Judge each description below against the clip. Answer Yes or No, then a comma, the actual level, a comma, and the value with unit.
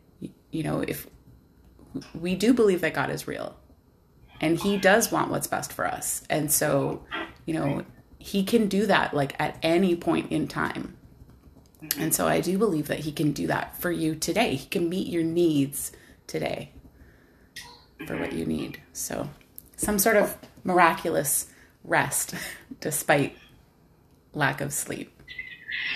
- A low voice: No, medium, 170 Hz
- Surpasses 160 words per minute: No, average, 150 wpm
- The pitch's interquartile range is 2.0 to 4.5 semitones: No, wide, 5.4 semitones